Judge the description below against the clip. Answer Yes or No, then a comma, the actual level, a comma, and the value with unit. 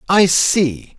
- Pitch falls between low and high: Yes, medium, 170 Hz